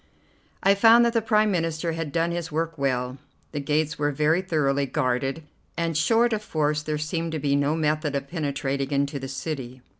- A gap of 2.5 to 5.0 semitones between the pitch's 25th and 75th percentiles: Yes, average, 3.0 semitones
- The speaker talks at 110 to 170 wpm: No, average, 190 wpm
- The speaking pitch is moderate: Yes, medium, 155 Hz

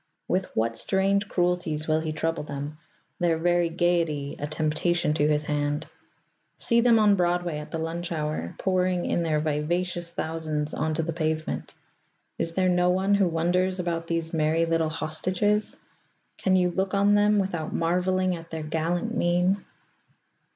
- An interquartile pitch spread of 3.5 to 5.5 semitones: No, average, 2.7 semitones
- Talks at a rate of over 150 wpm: Yes, average, 160 wpm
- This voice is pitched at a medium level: Yes, medium, 170 Hz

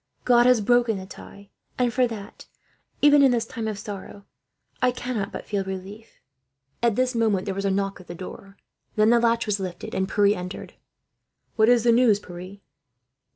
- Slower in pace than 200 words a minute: Yes, average, 190 wpm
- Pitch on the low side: No, high, 215 Hz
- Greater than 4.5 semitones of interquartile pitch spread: No, average, 3.4 semitones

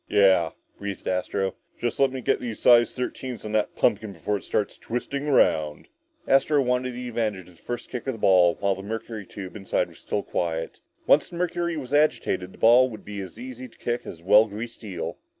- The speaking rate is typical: No, fast, 215 wpm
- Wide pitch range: No, average, 4.6 semitones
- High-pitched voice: No, low, 110 Hz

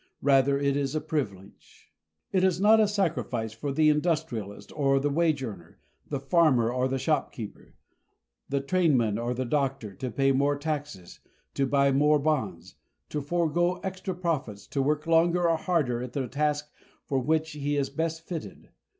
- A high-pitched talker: No, medium, 145 Hz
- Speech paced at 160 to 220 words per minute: Yes, average, 165 wpm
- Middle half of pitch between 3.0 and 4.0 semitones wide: Yes, average, 3.6 semitones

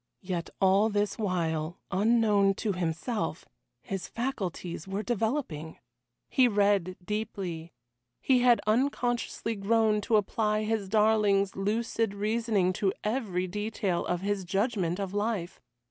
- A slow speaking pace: Yes, slow, 120 wpm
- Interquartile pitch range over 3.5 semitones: No, average, 3.1 semitones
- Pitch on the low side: No, high, 205 Hz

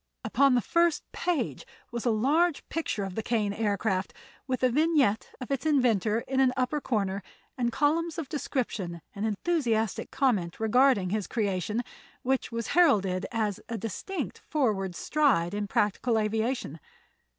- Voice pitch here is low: No, high, 230 Hz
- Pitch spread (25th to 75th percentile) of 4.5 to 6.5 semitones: Yes, average, 5.2 semitones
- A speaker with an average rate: Yes, average, 150 wpm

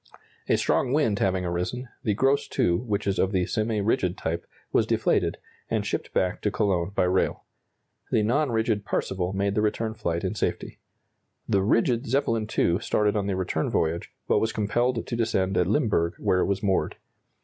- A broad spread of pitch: No, average, 3.5 semitones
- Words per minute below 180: No, average, 185 wpm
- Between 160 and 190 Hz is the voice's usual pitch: No, low, 100 Hz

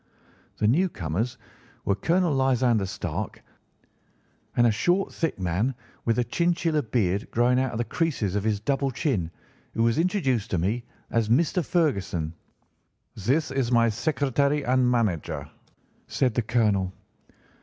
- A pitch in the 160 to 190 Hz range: No, low, 120 Hz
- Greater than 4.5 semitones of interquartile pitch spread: Yes, average, 5.0 semitones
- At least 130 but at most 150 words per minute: Yes, average, 140 wpm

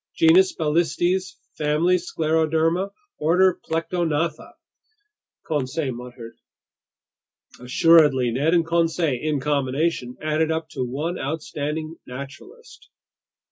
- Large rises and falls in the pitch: No, average, 3.1 semitones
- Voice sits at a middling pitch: Yes, medium, 160 Hz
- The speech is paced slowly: Yes, slow, 90 wpm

